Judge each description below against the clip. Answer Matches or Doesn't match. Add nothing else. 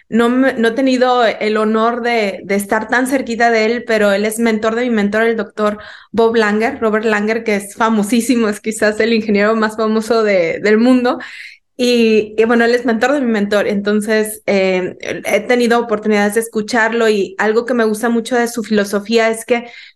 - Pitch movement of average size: Doesn't match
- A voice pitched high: Matches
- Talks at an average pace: Matches